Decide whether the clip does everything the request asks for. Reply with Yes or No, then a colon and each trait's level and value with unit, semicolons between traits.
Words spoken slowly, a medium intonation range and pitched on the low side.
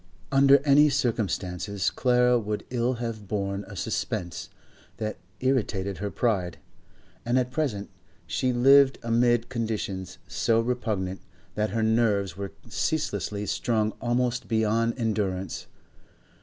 Yes: slow, 115 wpm; average, 3.6 semitones; low, 115 Hz